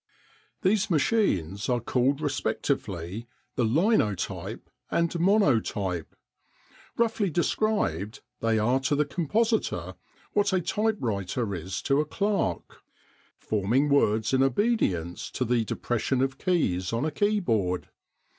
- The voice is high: No, low, 135 Hz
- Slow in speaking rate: Yes, slow, 115 wpm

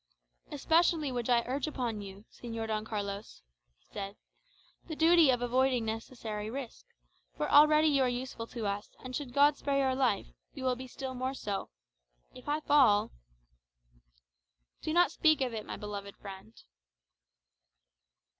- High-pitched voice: Yes, high, 245 Hz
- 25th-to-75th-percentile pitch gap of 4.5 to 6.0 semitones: Yes, average, 5.0 semitones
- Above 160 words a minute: No, average, 155 wpm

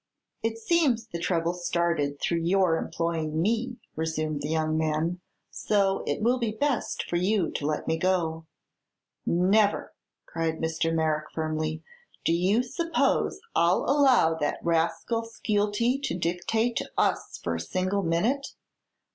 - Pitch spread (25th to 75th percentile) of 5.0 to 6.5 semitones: Yes, wide, 5.4 semitones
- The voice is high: No, medium, 175 Hz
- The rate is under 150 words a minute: Yes, average, 140 wpm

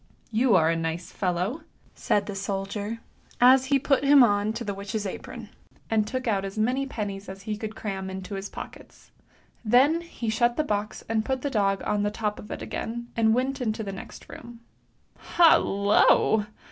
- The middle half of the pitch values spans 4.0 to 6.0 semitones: No, average, 3.5 semitones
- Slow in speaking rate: No, average, 195 wpm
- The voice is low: No, high, 215 Hz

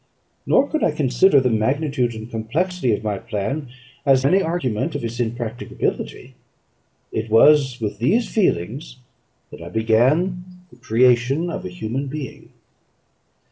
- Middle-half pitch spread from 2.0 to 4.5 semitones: No, average, 5.3 semitones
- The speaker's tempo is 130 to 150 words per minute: Yes, average, 140 wpm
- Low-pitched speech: Yes, low, 125 Hz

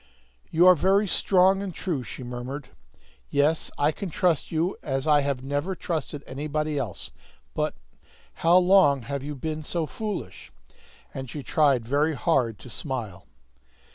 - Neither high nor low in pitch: Yes, medium, 150 Hz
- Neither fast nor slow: Yes, average, 150 wpm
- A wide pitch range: No, average, 4.2 semitones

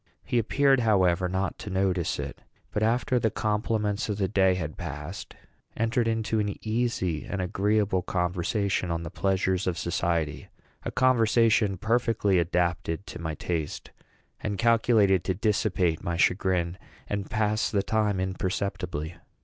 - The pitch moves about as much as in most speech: Yes, average, 3.7 semitones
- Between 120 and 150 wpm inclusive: Yes, average, 140 wpm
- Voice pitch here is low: Yes, very low, 95 Hz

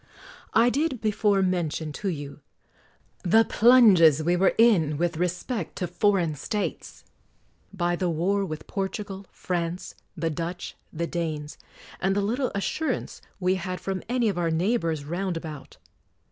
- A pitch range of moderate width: Yes, average, 3.7 semitones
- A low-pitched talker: No, medium, 180 Hz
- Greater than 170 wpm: No, average, 145 wpm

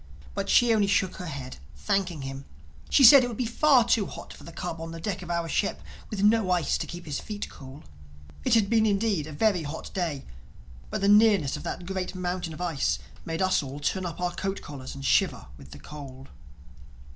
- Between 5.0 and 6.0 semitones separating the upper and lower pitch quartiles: Yes, average, 5.3 semitones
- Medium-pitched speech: Yes, medium, 180 Hz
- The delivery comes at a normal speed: No, fast, 220 wpm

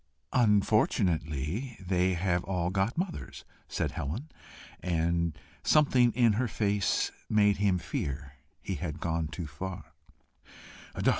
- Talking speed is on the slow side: Yes, slow, 115 wpm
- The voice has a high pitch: No, very low, 95 Hz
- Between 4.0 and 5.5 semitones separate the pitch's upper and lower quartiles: Yes, average, 4.4 semitones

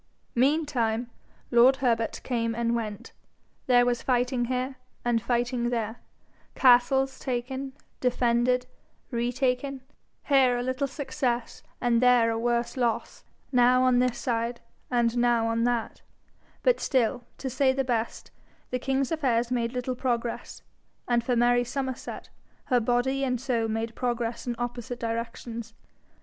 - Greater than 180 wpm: No, slow, 135 wpm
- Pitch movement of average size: No, narrow, 1.6 semitones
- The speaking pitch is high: Yes, high, 245 Hz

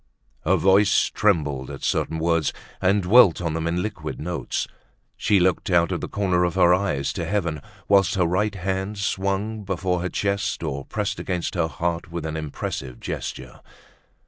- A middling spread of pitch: Yes, average, 3.3 semitones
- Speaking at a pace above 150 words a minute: Yes, average, 170 wpm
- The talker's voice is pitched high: No, very low, 90 Hz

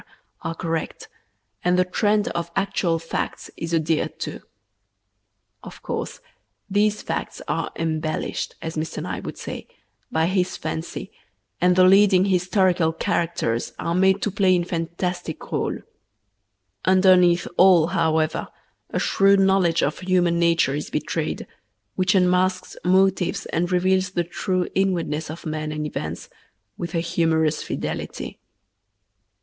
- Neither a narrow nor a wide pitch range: No, narrow, 2.3 semitones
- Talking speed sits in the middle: No, slow, 130 wpm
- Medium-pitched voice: Yes, medium, 180 Hz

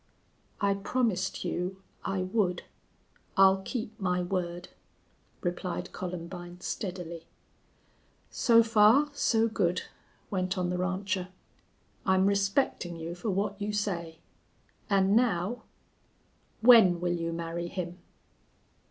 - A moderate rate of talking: No, slow, 110 wpm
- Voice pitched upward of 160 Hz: Yes, medium, 185 Hz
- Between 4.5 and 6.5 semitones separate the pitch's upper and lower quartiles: No, average, 2.7 semitones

